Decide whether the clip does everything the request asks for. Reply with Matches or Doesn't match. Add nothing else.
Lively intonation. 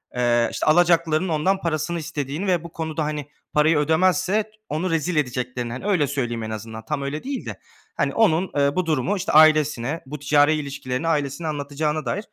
Doesn't match